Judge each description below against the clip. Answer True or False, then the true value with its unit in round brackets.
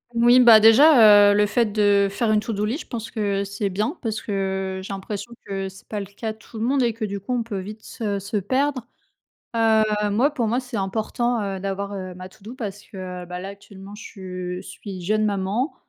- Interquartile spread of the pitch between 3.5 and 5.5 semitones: False (2.7 semitones)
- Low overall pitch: False (210 Hz)